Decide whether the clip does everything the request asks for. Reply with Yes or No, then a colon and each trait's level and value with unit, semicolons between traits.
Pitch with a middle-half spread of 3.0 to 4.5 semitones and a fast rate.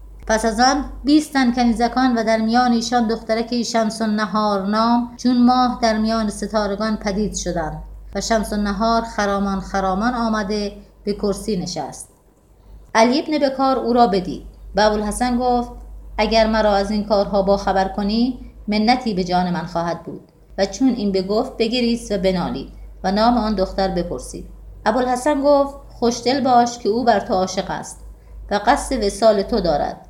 Yes: average, 3.3 semitones; fast, 160 wpm